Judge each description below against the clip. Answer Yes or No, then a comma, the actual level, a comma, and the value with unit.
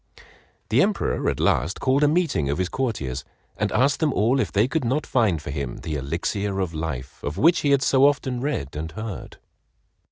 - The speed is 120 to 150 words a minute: No, average, 200 wpm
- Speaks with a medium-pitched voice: No, low, 105 Hz